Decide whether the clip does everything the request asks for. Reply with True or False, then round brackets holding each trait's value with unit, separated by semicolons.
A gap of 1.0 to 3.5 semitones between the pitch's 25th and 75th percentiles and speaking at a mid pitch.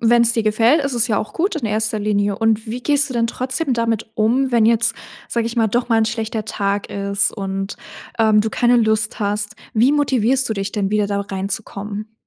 False (2.4 semitones; 220 Hz)